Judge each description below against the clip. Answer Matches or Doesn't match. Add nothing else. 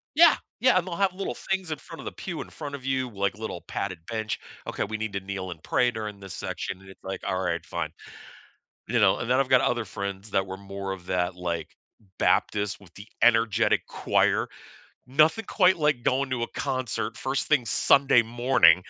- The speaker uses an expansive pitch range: Matches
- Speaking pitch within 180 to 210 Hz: Doesn't match